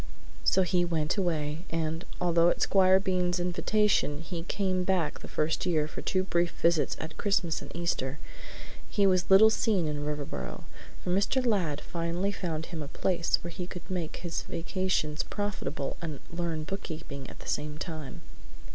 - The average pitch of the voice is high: No, medium, 170 Hz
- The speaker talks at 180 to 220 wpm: No, average, 165 wpm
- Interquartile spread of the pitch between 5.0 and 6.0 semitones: No, average, 3.2 semitones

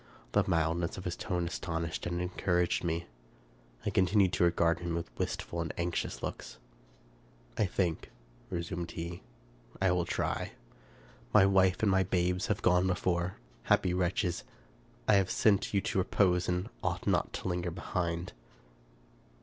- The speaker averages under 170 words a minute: Yes, average, 160 wpm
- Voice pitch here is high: No, very low, 90 Hz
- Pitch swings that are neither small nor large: No, narrow, 1.7 semitones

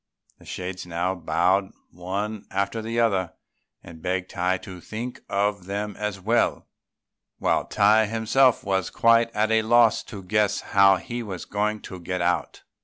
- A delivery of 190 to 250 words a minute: No, average, 160 wpm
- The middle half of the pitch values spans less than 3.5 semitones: Yes, average, 3.1 semitones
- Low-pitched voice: Yes, low, 100 Hz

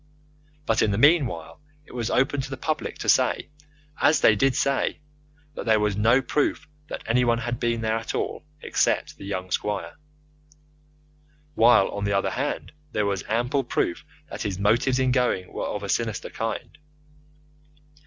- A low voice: Yes, low, 115 Hz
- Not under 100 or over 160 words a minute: No, average, 170 wpm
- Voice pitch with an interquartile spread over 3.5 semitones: Yes, average, 3.9 semitones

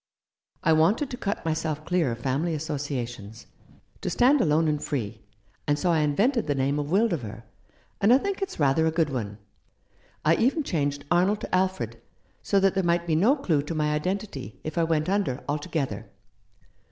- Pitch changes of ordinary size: Yes, average, 5.0 semitones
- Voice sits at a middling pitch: Yes, medium, 160 Hz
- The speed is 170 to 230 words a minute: Yes, average, 185 wpm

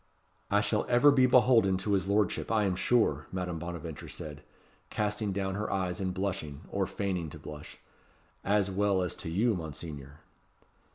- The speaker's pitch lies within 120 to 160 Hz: No, very low, 95 Hz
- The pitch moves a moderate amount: Yes, average, 3.5 semitones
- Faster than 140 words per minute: Yes, average, 165 wpm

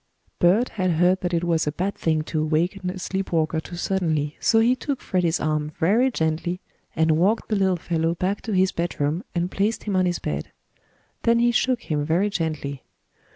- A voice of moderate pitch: Yes, medium, 175 Hz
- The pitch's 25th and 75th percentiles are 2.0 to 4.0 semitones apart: Yes, average, 3.5 semitones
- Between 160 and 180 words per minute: No, average, 200 wpm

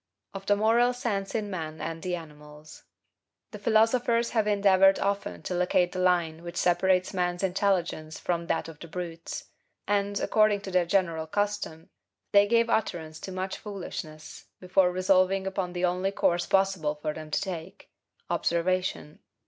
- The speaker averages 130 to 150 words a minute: No, average, 165 wpm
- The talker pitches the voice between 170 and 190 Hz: Yes, medium, 185 Hz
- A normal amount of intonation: Yes, average, 3.1 semitones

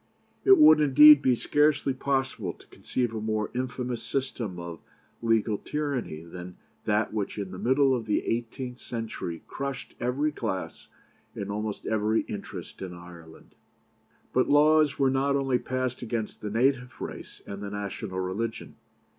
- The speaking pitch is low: Yes, low, 120 Hz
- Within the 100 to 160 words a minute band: Yes, average, 150 wpm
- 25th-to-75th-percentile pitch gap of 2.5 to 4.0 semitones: No, average, 4.7 semitones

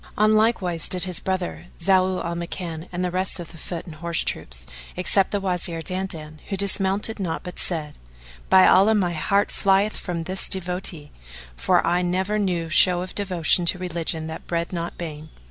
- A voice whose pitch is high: No, medium, 180 Hz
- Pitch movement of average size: No, narrow, 2.2 semitones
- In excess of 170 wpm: Yes, average, 185 wpm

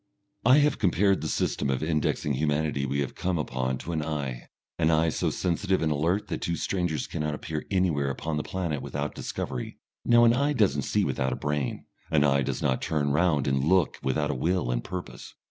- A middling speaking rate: No, fast, 210 wpm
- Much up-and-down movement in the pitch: No, average, 4.4 semitones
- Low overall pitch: Yes, very low, 75 Hz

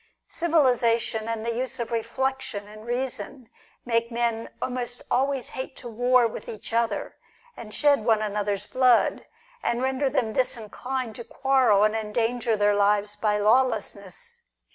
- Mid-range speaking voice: No, high, 235 Hz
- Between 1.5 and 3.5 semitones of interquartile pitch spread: Yes, average, 3.1 semitones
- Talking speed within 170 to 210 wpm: No, average, 140 wpm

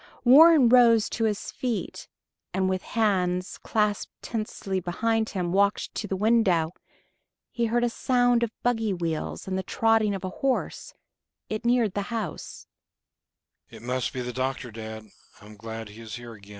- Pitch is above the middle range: Yes, high, 210 Hz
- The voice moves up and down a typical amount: Yes, average, 4.4 semitones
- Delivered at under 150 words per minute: Yes, average, 140 wpm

